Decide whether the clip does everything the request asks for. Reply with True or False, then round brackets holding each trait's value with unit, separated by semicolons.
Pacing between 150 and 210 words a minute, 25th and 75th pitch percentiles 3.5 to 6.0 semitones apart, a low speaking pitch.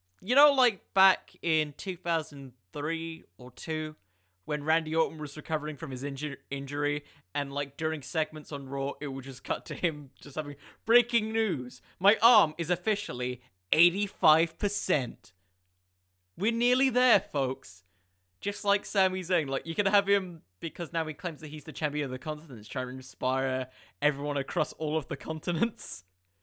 False (170 wpm; 5.1 semitones; 150 Hz)